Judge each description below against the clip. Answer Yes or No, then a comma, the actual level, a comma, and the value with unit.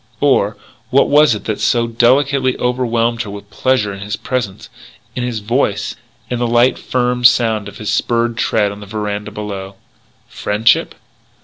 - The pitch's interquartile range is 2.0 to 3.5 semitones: Yes, average, 3.0 semitones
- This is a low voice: Yes, low, 115 Hz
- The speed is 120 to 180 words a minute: Yes, average, 165 wpm